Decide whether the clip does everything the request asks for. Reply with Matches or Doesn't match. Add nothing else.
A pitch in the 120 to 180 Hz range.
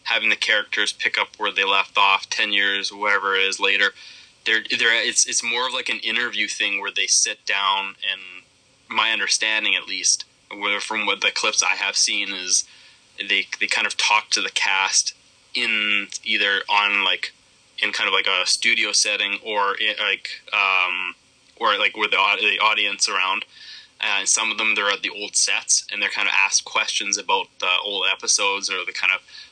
Doesn't match